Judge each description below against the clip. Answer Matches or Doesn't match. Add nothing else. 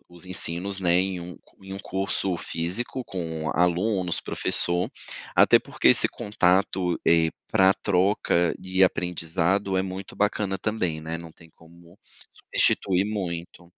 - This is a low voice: Matches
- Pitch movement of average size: Doesn't match